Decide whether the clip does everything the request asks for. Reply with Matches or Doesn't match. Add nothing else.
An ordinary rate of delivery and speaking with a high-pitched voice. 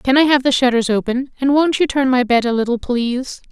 Doesn't match